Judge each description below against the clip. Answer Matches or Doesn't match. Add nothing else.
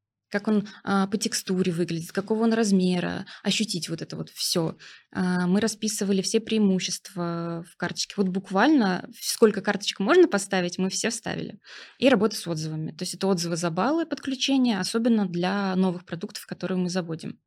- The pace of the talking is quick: Matches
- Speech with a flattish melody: Doesn't match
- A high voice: Matches